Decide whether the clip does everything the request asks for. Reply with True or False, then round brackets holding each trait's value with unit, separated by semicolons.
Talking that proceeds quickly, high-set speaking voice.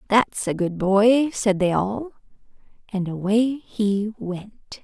False (135 wpm; 210 Hz)